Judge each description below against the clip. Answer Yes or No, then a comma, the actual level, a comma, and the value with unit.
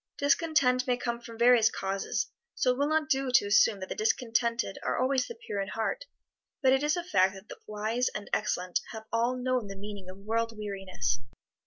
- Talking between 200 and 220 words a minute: Yes, fast, 205 wpm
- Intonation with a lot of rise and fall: No, average, 4.3 semitones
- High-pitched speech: Yes, high, 230 Hz